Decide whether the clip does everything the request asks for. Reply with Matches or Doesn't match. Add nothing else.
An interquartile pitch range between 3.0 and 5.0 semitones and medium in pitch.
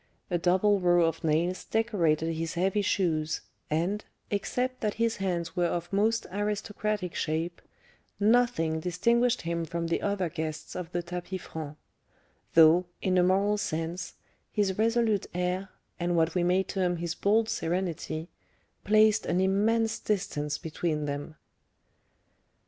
Matches